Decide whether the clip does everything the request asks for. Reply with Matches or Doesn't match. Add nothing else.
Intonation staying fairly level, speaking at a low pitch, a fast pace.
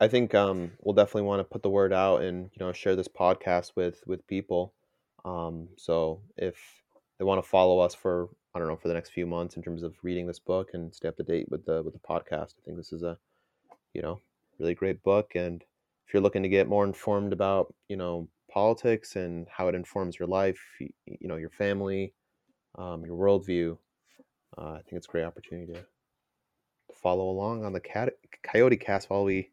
Matches